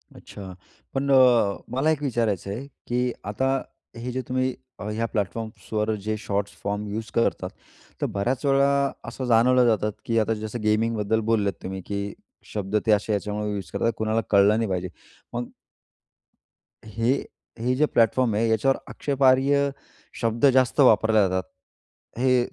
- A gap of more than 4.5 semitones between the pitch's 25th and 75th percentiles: No, average, 3.5 semitones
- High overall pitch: No, low, 115 Hz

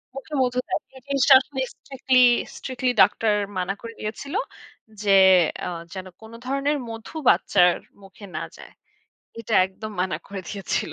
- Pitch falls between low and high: No, high, 225 Hz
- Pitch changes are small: No, average, 5.3 semitones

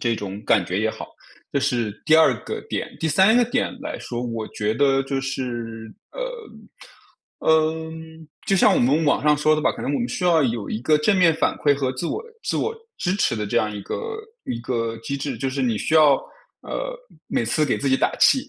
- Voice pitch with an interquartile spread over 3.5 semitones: Yes, wide, 5.5 semitones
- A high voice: No, medium, 140 Hz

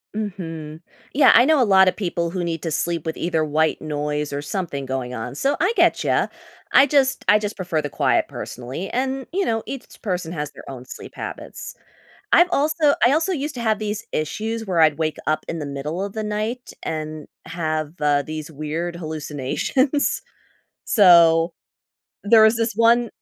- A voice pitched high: No, medium, 175 Hz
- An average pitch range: No, wide, 6.8 semitones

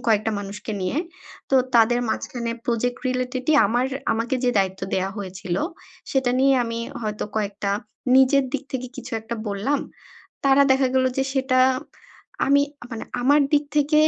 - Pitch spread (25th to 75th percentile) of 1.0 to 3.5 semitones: No, average, 3.9 semitones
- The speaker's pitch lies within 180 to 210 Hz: No, high, 245 Hz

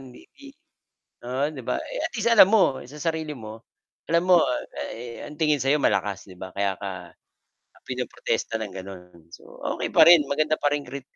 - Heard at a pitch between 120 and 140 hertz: Yes, low, 135 Hz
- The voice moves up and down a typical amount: No, wide, 7.5 semitones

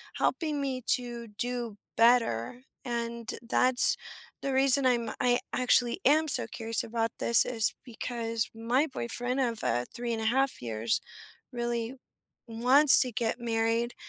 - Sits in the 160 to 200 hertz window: No, high, 240 Hz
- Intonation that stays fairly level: Yes, narrow, 1.8 semitones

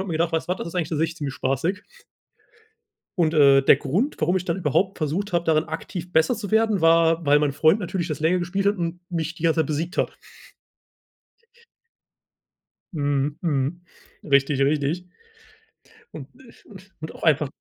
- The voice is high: No, medium, 165 Hz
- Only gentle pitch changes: No, average, 3.2 semitones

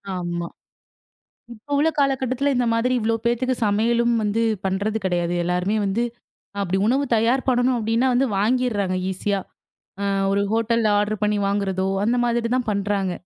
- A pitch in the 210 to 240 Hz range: Yes, high, 220 Hz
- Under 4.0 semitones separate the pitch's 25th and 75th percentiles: Yes, average, 3.5 semitones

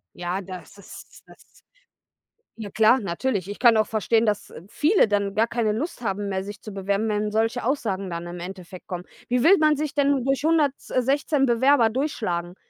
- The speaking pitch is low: No, high, 220 Hz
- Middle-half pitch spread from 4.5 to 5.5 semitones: Yes, average, 5.2 semitones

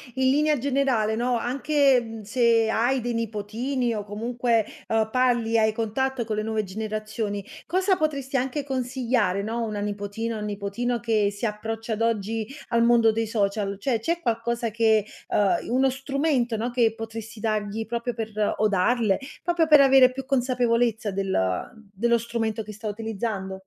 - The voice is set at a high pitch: Yes, high, 230 Hz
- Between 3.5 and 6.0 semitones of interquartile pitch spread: No, average, 2.7 semitones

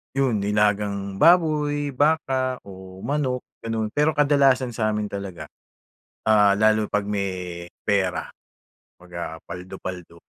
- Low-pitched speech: Yes, low, 105 Hz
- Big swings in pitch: Yes, wide, 5.7 semitones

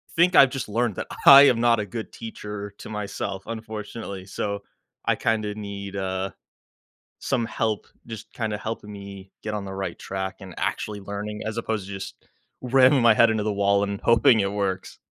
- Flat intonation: Yes, narrow, 2.3 semitones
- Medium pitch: No, low, 105 Hz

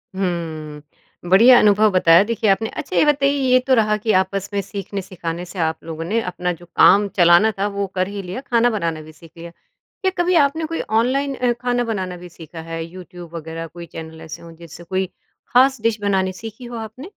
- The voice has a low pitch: No, high, 190 Hz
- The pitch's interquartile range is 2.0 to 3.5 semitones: No, average, 5.2 semitones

